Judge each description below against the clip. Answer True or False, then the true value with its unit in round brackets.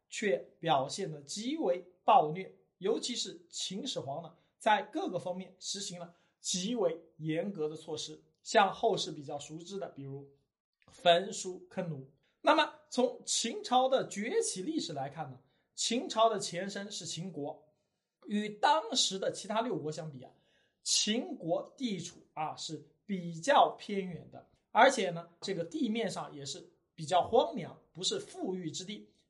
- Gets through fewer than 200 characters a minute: False (220 characters per minute)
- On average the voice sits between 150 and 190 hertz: True (185 Hz)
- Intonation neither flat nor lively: False (5.7 semitones)